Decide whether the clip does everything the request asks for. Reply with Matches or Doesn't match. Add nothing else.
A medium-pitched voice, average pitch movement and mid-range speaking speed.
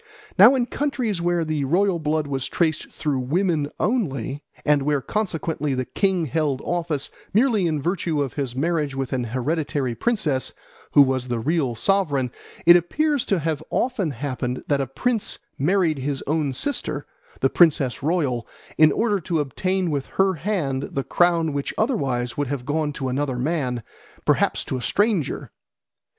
Matches